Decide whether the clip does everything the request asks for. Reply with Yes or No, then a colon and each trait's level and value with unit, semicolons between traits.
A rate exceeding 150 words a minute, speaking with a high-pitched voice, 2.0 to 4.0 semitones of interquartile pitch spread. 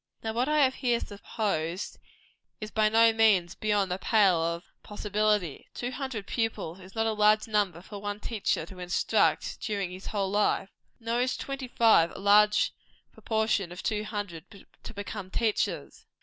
Yes: average, 165 wpm; high, 210 Hz; average, 2.7 semitones